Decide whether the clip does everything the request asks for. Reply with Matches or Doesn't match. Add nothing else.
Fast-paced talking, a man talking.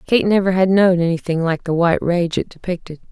Doesn't match